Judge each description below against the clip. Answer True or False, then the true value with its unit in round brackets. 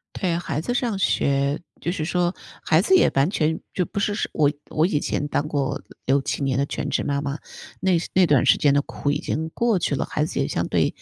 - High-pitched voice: False (155 Hz)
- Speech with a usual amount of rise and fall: True (4.0 semitones)